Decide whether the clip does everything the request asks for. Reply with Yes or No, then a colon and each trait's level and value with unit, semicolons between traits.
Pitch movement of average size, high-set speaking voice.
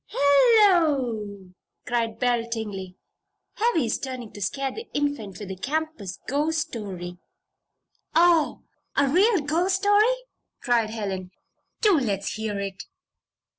No: wide, 7.7 semitones; very high, 250 Hz